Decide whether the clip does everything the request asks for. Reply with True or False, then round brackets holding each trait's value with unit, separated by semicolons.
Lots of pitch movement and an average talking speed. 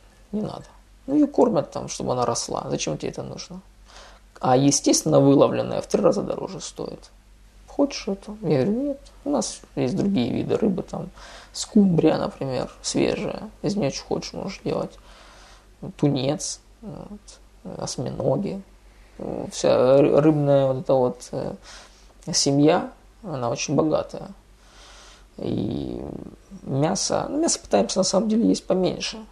True (7.8 semitones; 130 wpm)